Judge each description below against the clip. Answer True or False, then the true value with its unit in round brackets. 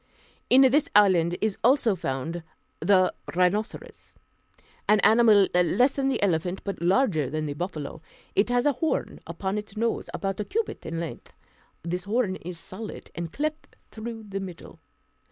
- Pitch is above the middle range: True (200 Hz)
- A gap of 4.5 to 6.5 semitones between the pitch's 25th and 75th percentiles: True (5.1 semitones)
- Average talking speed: True (155 wpm)